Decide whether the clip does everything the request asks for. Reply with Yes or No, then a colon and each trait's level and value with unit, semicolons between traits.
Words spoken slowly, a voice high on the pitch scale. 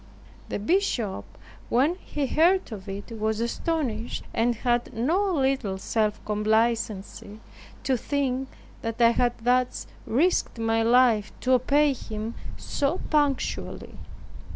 Yes: slow, 120 wpm; high, 240 Hz